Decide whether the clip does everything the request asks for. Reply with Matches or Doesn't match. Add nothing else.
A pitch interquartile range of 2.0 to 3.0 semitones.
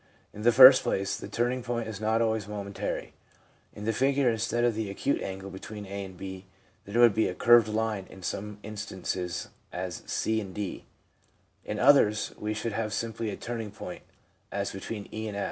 Matches